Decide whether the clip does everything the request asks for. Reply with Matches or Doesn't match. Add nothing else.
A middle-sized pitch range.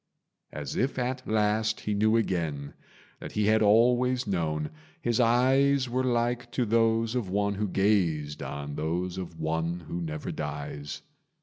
Doesn't match